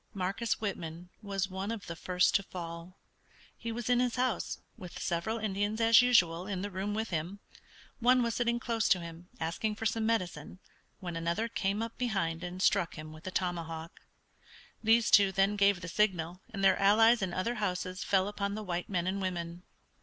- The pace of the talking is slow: No, average, 190 wpm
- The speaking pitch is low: No, high, 195 Hz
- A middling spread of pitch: Yes, average, 3.9 semitones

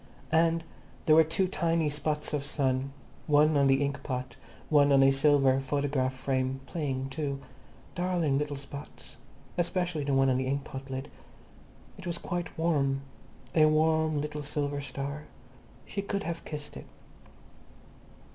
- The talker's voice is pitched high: No, medium, 145 Hz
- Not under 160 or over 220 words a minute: No, average, 145 wpm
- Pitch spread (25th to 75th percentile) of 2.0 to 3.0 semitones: Yes, narrow, 2.6 semitones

